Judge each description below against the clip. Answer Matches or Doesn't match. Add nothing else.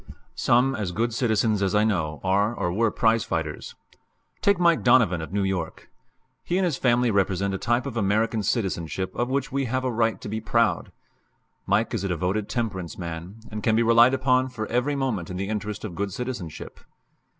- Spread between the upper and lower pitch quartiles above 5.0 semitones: Doesn't match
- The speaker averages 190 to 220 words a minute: Matches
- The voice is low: Matches